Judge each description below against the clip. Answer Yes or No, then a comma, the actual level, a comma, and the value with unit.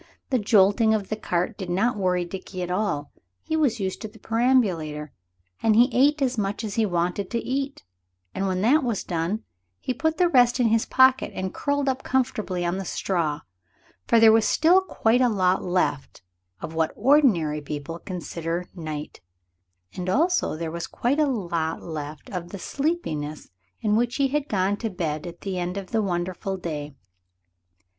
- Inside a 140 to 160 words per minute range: No, average, 180 wpm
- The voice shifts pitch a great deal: Yes, wide, 5.9 semitones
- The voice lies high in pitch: Yes, high, 195 Hz